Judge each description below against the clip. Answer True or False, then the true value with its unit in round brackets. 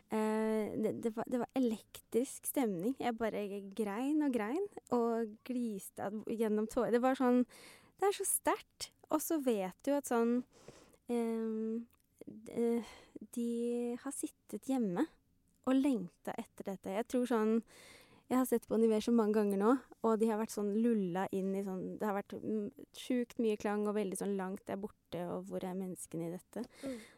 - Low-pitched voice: False (230 Hz)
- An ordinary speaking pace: True (170 wpm)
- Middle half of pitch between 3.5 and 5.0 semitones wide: False (2.9 semitones)